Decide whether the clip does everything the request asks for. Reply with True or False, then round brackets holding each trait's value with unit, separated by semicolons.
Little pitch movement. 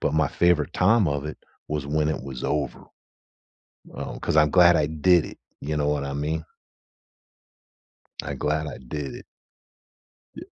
True (1.4 semitones)